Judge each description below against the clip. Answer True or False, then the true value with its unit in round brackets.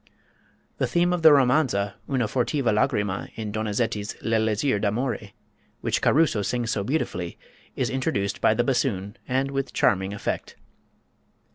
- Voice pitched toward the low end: True (115 Hz)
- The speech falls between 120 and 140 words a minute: True (135 wpm)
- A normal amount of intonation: True (4.8 semitones)